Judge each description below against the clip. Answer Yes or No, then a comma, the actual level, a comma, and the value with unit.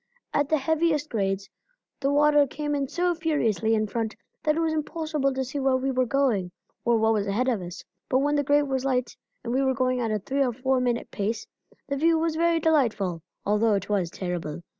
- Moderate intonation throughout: Yes, average, 5.0 semitones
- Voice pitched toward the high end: Yes, very high, 260 Hz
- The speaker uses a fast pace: Yes, fast, 220 wpm